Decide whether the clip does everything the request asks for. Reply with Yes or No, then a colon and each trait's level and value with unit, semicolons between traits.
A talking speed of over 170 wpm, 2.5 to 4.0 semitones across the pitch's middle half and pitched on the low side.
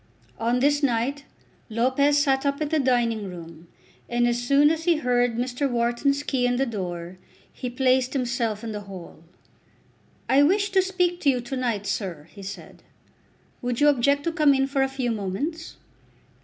No: average, 180 wpm; average, 3.6 semitones; very high, 255 Hz